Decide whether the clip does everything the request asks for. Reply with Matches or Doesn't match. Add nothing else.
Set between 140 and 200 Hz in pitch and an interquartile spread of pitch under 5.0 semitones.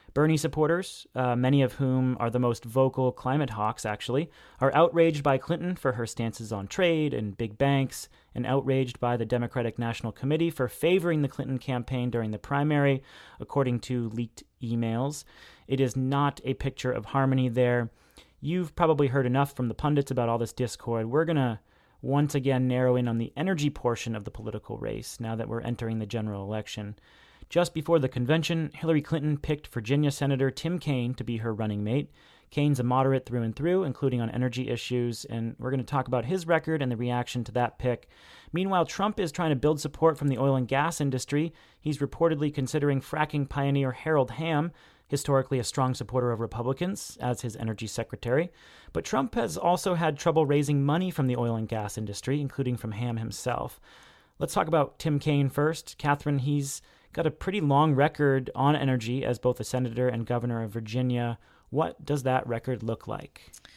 Doesn't match